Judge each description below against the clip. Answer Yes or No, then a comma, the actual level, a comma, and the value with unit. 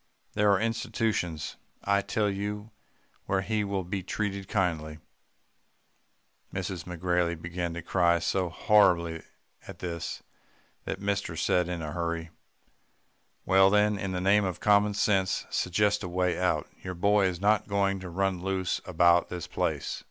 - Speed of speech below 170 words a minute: Yes, average, 150 wpm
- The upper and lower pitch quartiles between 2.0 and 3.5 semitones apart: Yes, average, 2.7 semitones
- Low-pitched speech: Yes, very low, 95 Hz